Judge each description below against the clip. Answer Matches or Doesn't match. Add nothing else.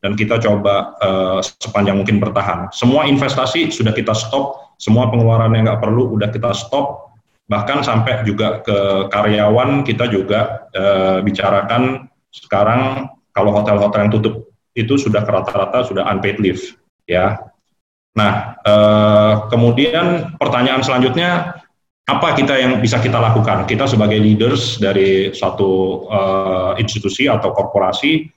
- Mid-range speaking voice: Doesn't match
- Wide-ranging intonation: Doesn't match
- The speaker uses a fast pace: Doesn't match